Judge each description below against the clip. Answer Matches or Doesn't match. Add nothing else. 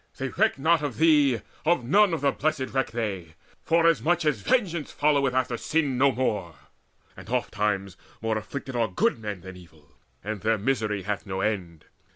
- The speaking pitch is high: Doesn't match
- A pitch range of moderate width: Doesn't match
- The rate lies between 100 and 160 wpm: Doesn't match